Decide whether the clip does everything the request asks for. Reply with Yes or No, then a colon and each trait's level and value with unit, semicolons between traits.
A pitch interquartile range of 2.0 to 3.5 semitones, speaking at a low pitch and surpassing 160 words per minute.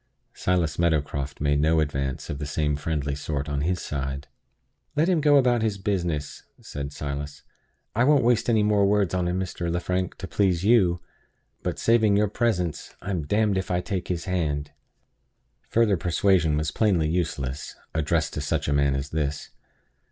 No: wide, 5.5 semitones; very low, 85 Hz; average, 175 wpm